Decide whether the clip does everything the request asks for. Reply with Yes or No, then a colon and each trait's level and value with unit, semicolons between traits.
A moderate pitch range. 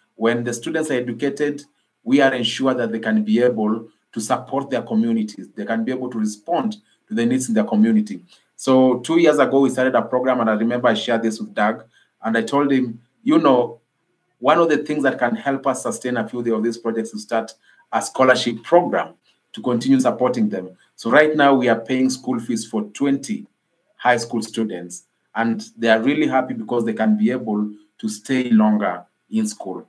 Yes: average, 4.3 semitones